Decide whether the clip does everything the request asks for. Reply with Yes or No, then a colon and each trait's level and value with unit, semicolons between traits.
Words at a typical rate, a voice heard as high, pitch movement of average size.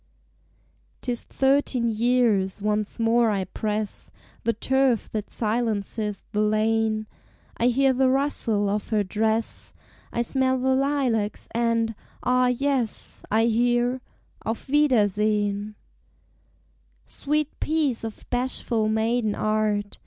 No: slow, 110 wpm; high, 230 Hz; average, 3.0 semitones